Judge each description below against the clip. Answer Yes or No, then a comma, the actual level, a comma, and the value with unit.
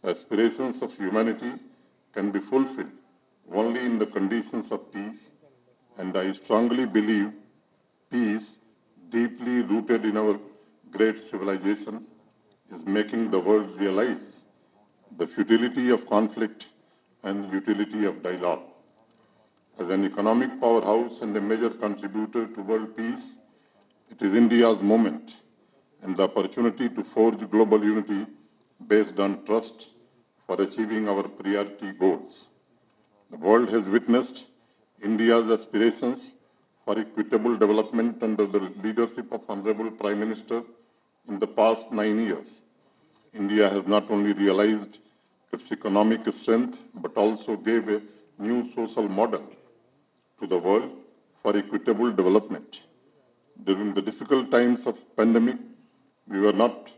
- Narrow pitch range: Yes, narrow, 2.0 semitones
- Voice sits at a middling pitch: No, low, 110 Hz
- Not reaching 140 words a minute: Yes, average, 125 wpm